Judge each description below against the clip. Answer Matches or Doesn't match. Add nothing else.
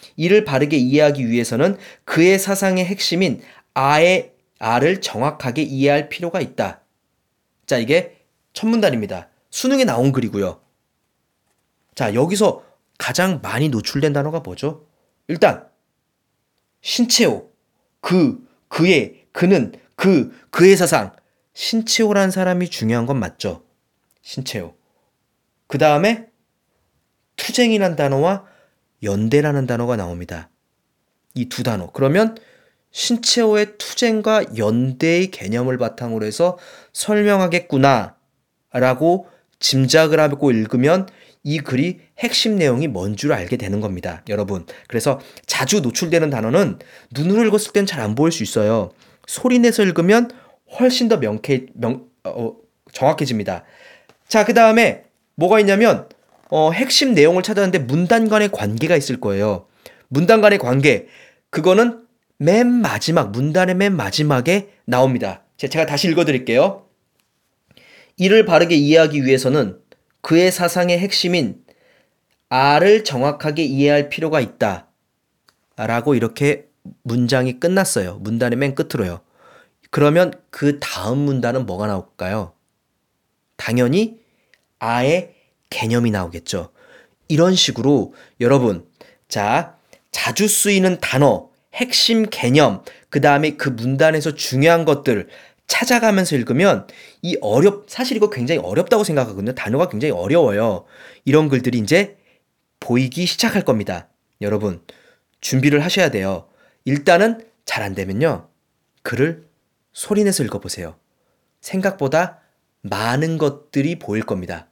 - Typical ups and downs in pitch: Doesn't match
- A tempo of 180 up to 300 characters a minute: Matches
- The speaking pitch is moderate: Matches